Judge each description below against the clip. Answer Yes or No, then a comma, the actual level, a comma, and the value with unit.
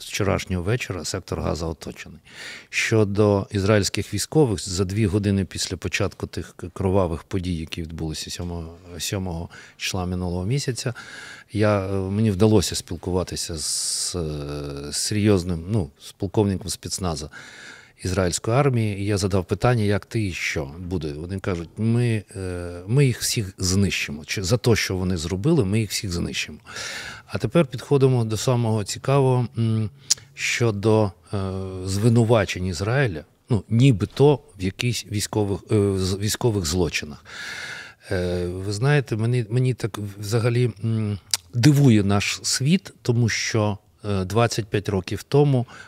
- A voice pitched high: No, low, 105 Hz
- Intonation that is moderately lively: Yes, average, 4.0 semitones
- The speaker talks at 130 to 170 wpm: No, average, 120 wpm